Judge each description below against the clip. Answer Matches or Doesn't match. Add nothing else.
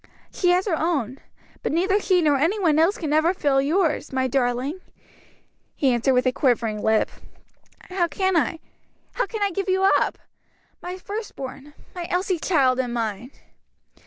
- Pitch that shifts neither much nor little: Doesn't match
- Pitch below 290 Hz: Doesn't match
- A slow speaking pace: Doesn't match